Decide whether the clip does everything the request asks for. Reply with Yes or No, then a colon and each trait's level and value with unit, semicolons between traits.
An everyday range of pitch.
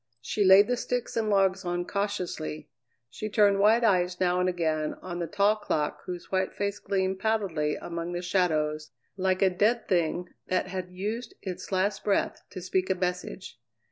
No: narrow, 2.3 semitones